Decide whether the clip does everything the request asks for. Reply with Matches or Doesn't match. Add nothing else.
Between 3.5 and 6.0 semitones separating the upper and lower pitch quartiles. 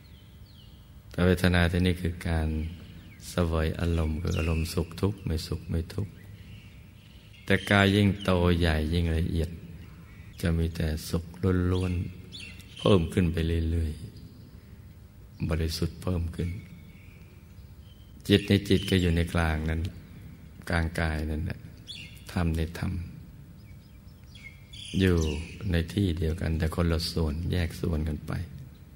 Doesn't match